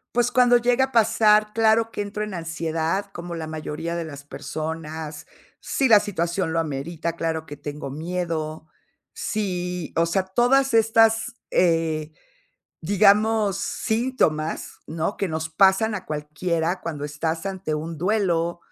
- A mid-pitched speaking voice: Yes, medium, 170 Hz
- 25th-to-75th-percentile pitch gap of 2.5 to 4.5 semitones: No, average, 4.9 semitones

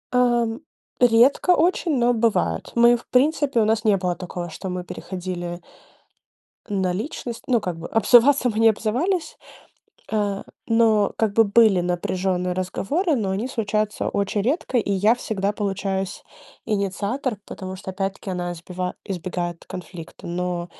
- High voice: Yes, high, 205 Hz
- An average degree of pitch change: Yes, average, 4.4 semitones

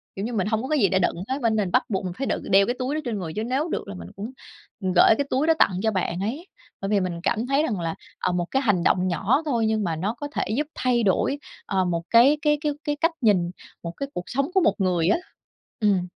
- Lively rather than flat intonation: Yes, wide, 6.5 semitones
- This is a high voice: Yes, high, 215 Hz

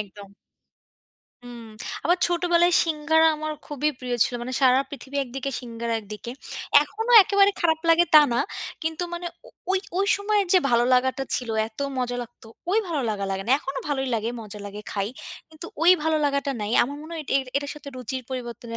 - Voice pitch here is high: Yes, very high, 275 Hz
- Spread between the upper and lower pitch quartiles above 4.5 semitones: Yes, average, 5.1 semitones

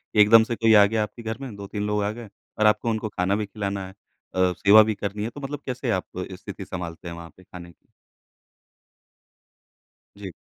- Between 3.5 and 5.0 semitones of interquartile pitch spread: No, average, 2.8 semitones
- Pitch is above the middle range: No, low, 105 Hz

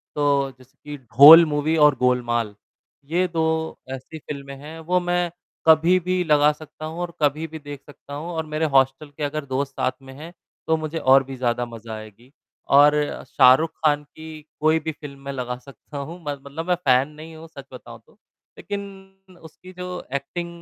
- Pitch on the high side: No, medium, 150 Hz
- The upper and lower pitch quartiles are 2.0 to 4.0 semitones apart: Yes, average, 3.1 semitones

